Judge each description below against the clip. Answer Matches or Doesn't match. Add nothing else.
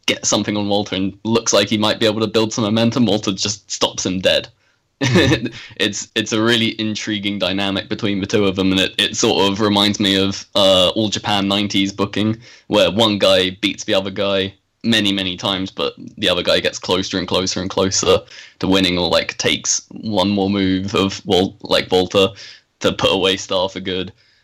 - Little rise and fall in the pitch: Matches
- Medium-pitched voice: Doesn't match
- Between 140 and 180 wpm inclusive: Doesn't match